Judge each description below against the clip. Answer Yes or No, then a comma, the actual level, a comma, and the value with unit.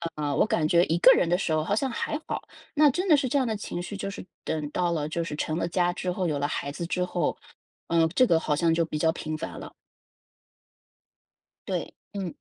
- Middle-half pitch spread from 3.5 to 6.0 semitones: Yes, average, 4.0 semitones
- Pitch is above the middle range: No, medium, 170 Hz